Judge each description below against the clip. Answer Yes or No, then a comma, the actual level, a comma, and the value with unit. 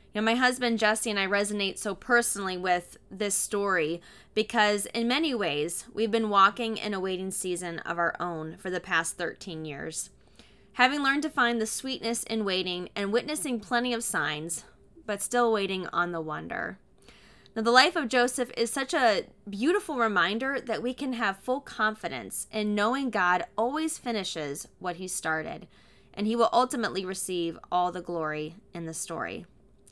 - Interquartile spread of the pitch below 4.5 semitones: No, average, 4.9 semitones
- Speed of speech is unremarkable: Yes, average, 170 wpm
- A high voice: Yes, high, 210 Hz